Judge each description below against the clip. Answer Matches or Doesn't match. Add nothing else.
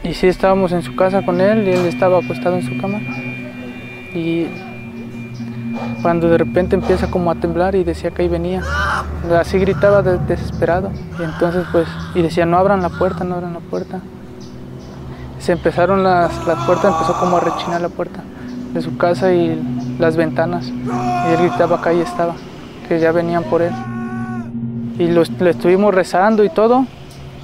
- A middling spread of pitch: Doesn't match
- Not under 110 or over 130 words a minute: Doesn't match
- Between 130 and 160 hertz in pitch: Doesn't match